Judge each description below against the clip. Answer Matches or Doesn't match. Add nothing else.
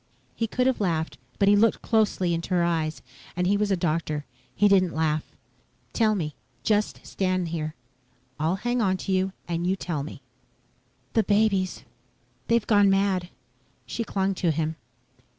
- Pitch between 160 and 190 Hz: Matches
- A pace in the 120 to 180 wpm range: Matches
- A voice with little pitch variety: Doesn't match